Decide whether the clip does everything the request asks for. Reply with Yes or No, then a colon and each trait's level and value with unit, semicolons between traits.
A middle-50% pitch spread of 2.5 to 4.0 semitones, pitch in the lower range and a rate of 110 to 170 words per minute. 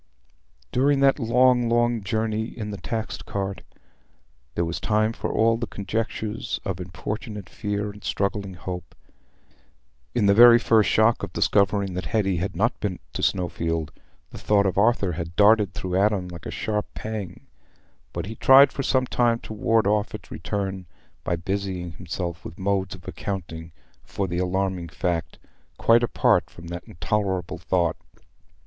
Yes: average, 3.6 semitones; low, 100 Hz; average, 160 wpm